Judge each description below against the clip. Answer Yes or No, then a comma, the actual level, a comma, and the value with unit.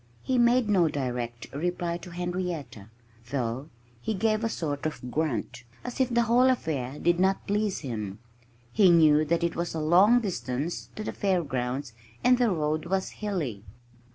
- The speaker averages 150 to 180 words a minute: Yes, average, 165 wpm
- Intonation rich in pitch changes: Yes, wide, 6.8 semitones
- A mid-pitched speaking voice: Yes, medium, 170 Hz